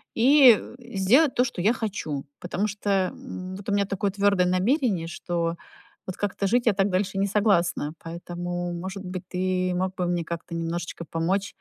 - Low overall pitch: No, high, 190 Hz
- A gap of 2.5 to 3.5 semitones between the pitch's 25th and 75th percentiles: Yes, average, 2.8 semitones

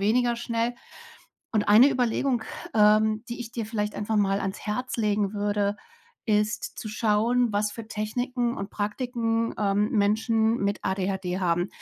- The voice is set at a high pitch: Yes, high, 215 Hz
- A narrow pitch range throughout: Yes, narrow, 2.2 semitones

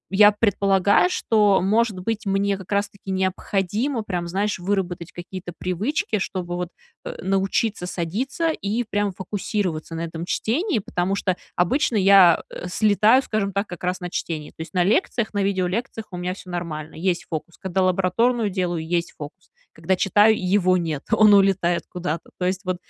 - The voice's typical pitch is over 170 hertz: Yes, high, 190 Hz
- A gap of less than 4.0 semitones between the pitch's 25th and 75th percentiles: Yes, average, 2.7 semitones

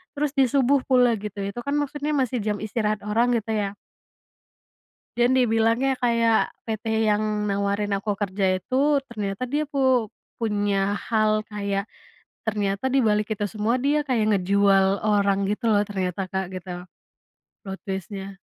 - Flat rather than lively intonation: No, average, 3.5 semitones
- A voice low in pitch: No, high, 215 Hz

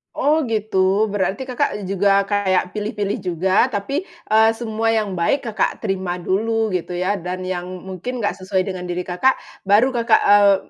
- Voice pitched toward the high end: Yes, high, 200 Hz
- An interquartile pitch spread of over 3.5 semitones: No, average, 2.9 semitones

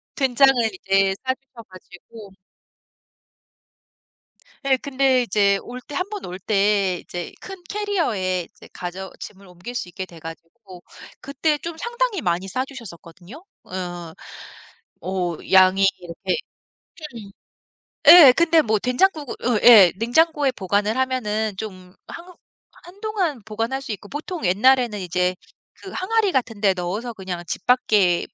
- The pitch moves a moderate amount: No, wide, 6.7 semitones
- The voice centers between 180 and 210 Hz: No, high, 220 Hz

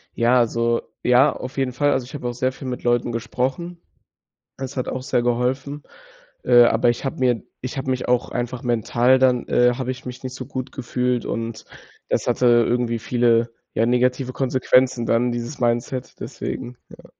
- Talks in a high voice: No, low, 125 Hz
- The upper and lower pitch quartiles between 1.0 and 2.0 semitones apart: Yes, narrow, 1.3 semitones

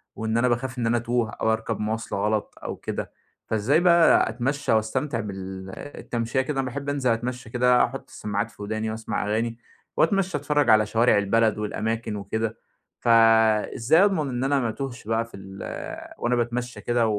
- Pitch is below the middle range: Yes, low, 115 Hz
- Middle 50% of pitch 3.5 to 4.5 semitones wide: No, average, 2.9 semitones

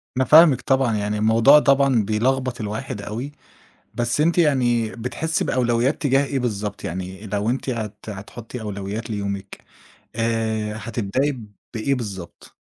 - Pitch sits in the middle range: No, low, 115 Hz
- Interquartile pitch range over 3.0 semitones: Yes, average, 3.9 semitones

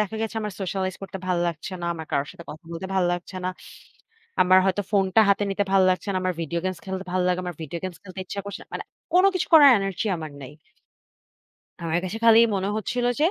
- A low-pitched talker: No, medium, 185 Hz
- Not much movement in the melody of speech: Yes, narrow, 2.3 semitones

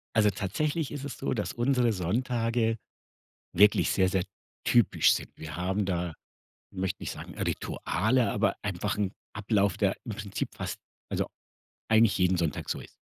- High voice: No, low, 105 Hz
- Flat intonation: No, average, 3.5 semitones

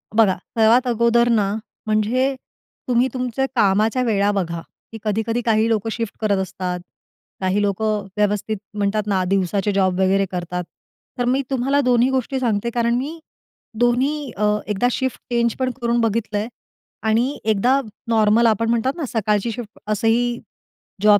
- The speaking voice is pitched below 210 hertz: No, high, 225 Hz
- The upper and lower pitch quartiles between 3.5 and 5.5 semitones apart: No, average, 3.0 semitones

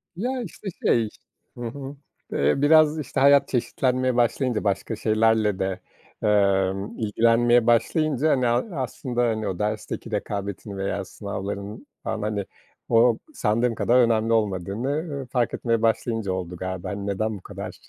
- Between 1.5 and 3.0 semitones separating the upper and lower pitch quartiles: No, average, 3.9 semitones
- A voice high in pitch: No, low, 115 Hz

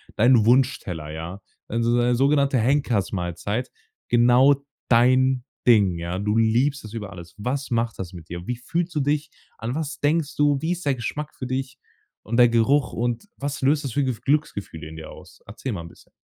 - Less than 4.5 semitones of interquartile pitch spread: No, average, 5.1 semitones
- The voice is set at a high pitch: No, low, 120 Hz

